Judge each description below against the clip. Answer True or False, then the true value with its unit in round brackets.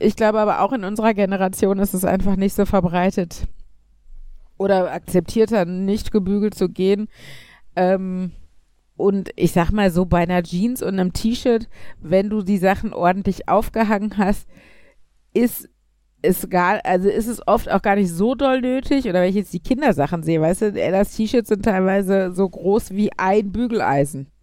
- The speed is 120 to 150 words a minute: False (170 wpm)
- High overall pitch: True (195 Hz)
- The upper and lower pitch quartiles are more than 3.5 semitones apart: False (2.9 semitones)